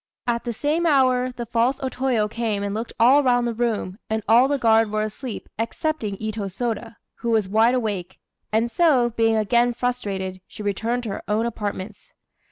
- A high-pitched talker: Yes, high, 230 Hz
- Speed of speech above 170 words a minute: Yes, average, 185 wpm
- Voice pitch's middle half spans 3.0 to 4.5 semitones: No, narrow, 2.6 semitones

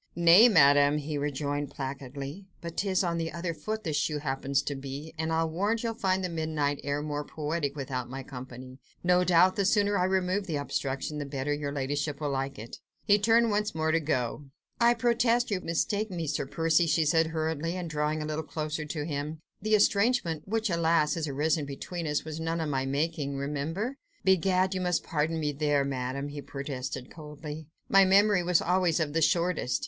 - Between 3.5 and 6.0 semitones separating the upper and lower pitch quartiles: Yes, average, 4.0 semitones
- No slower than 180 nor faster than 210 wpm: Yes, average, 195 wpm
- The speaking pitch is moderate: Yes, medium, 160 Hz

